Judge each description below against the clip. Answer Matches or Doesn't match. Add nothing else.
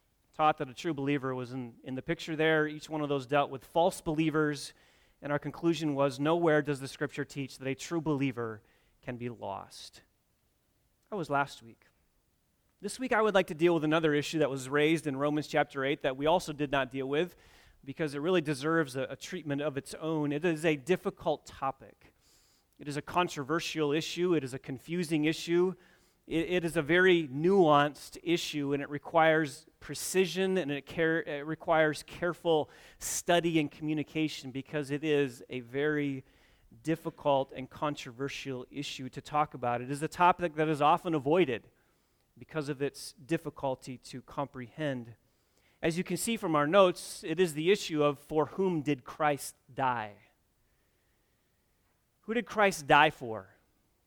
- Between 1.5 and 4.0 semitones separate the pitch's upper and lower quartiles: Matches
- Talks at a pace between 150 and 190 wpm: Matches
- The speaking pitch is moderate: Matches